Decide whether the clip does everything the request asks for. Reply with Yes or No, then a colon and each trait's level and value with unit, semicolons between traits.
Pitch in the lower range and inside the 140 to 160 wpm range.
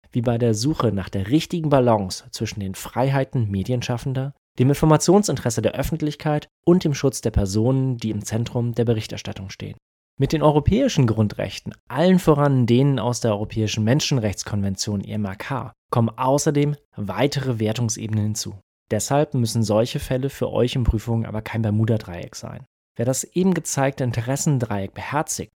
Yes: low, 120 Hz; average, 145 wpm